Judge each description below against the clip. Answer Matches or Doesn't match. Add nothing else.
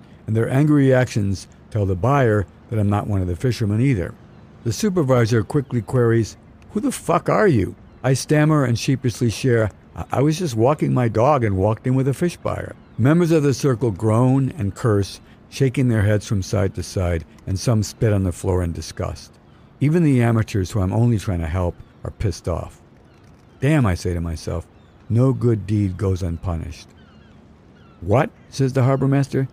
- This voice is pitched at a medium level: Doesn't match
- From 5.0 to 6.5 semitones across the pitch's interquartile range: Matches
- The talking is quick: Doesn't match